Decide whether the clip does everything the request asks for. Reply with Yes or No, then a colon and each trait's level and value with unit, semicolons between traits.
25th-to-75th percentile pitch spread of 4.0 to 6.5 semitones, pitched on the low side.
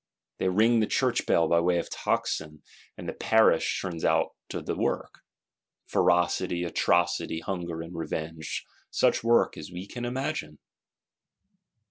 Yes: average, 5.0 semitones; very low, 90 Hz